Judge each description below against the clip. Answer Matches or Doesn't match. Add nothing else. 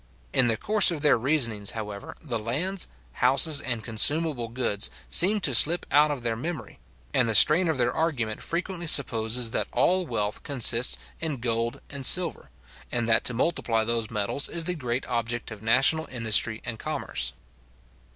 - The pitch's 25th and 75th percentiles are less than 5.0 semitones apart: Doesn't match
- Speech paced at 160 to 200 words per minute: Matches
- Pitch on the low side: Matches